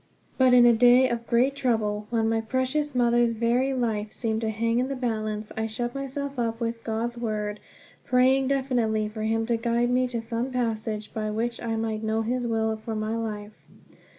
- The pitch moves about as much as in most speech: No, narrow, 2.1 semitones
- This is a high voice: Yes, high, 230 Hz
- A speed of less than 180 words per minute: No, average, 195 wpm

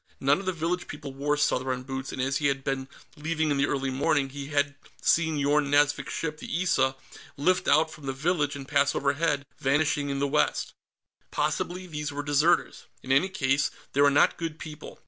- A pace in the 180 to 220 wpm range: Yes, average, 200 wpm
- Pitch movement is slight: Yes, narrow, 2.2 semitones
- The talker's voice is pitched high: No, medium, 145 Hz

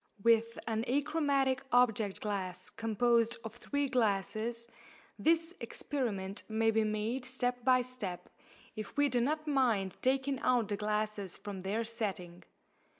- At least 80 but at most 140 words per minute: Yes, slow, 135 wpm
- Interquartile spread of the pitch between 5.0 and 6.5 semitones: No, average, 3.4 semitones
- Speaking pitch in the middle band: No, high, 230 Hz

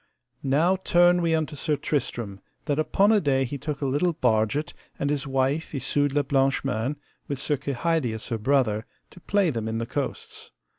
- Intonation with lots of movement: No, average, 3.9 semitones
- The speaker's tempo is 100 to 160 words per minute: No, average, 185 wpm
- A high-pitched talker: No, medium, 140 Hz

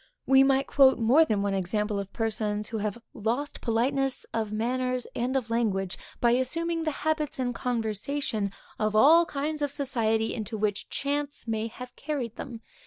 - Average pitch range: Yes, average, 4.2 semitones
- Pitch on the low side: No, high, 240 Hz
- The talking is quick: No, average, 170 wpm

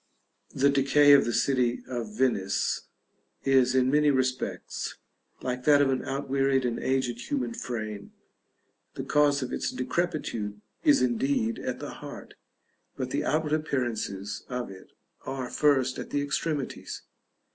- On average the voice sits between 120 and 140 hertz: Yes, low, 135 Hz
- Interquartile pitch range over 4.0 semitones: No, average, 2.9 semitones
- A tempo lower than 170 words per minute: Yes, average, 140 wpm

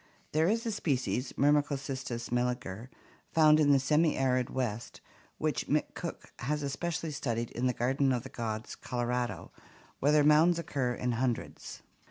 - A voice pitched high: No, low, 130 Hz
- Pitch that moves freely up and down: No, average, 3.5 semitones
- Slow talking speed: No, average, 150 wpm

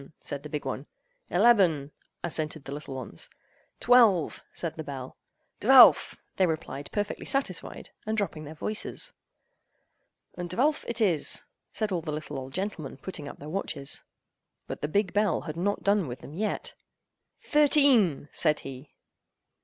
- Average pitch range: No, wide, 5.9 semitones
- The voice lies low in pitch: No, medium, 165 Hz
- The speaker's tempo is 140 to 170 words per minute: Yes, average, 150 wpm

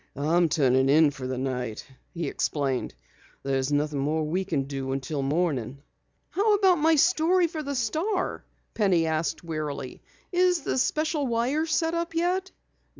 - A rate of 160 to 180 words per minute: No, average, 150 wpm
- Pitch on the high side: No, medium, 165 Hz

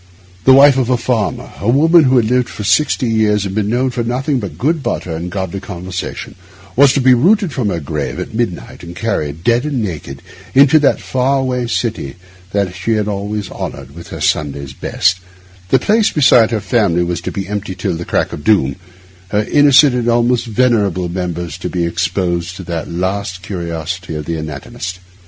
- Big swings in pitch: Yes, wide, 6.1 semitones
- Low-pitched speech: Yes, low, 105 Hz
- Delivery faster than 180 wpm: Yes, average, 195 wpm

